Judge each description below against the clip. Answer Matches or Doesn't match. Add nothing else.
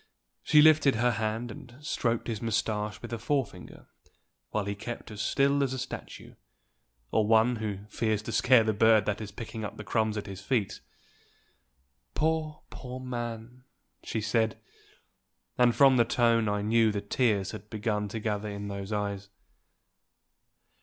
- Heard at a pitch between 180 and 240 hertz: Doesn't match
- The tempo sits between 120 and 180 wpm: Matches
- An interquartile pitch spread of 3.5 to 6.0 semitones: Doesn't match